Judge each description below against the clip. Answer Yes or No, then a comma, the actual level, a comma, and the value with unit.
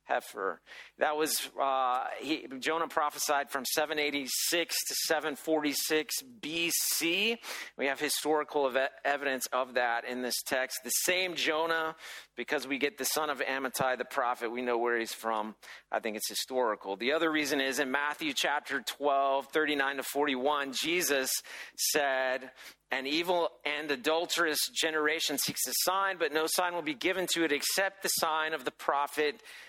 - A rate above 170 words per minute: No, average, 160 wpm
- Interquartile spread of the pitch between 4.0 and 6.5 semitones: No, average, 3.4 semitones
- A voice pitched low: No, medium, 150 Hz